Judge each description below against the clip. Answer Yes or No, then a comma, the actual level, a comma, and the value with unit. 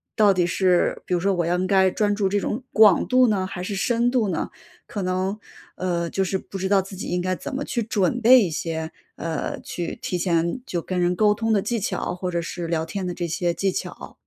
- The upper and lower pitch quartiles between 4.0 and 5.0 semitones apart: No, average, 2.9 semitones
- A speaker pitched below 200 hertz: Yes, high, 190 Hz